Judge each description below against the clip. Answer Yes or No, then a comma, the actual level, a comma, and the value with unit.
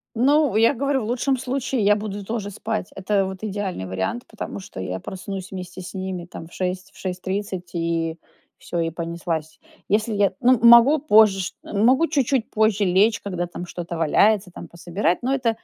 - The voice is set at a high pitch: Yes, high, 200 Hz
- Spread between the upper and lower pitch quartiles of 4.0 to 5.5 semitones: Yes, average, 4.3 semitones